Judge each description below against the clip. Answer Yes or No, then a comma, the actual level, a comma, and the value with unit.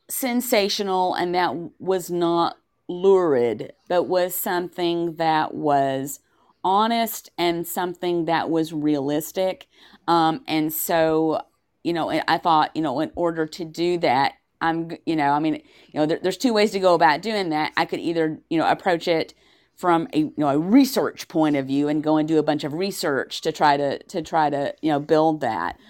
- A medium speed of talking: Yes, average, 190 wpm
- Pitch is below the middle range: No, medium, 165 Hz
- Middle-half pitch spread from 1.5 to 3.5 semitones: Yes, average, 2.9 semitones